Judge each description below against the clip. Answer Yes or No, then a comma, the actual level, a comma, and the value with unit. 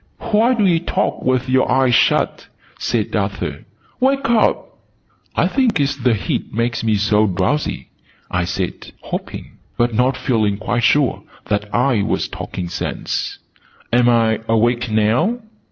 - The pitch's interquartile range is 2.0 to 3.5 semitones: No, average, 4.3 semitones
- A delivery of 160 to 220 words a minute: No, average, 145 wpm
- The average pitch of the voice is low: Yes, low, 120 Hz